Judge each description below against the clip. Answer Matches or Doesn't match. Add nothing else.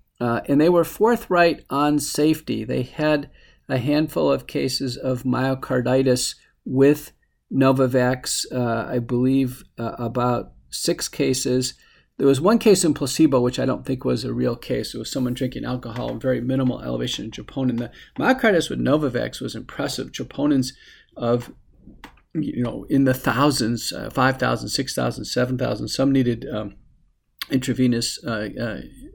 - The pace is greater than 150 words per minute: Doesn't match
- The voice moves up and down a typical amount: Doesn't match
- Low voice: Matches